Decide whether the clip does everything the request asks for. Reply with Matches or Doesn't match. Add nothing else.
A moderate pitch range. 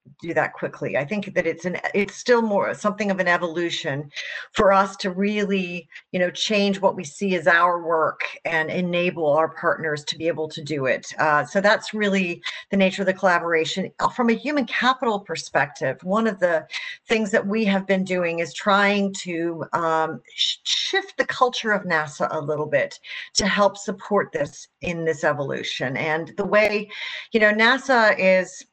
Matches